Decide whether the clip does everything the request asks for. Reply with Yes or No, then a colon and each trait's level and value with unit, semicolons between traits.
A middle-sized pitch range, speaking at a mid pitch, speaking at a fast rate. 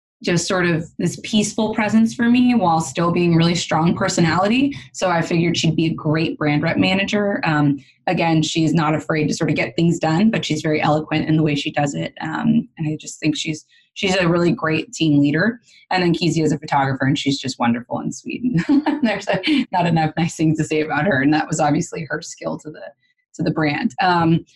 Yes: average, 3.6 semitones; medium, 165 Hz; fast, 220 wpm